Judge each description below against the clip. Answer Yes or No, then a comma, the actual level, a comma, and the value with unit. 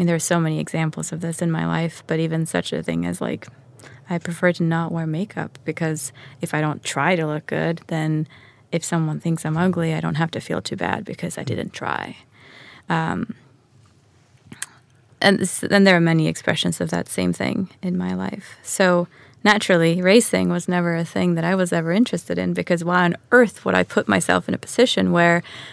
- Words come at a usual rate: No, fast, 210 wpm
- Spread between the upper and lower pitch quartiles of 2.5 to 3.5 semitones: No, average, 5.2 semitones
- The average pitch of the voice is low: No, medium, 160 Hz